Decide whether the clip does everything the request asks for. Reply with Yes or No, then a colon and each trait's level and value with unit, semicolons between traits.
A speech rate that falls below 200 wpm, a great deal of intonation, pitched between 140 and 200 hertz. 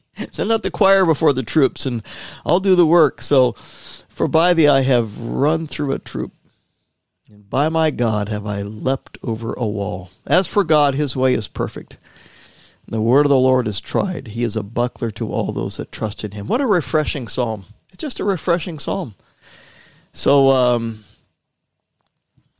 No: average, 180 wpm; wide, 6.3 semitones; low, 130 Hz